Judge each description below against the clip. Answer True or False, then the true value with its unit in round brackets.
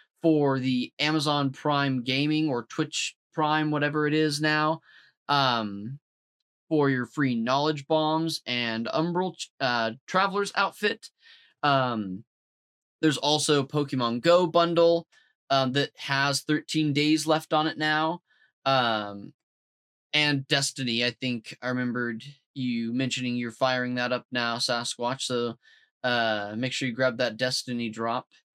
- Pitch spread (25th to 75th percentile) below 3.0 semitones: False (4.1 semitones)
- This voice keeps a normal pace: False (130 wpm)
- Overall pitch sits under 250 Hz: True (140 Hz)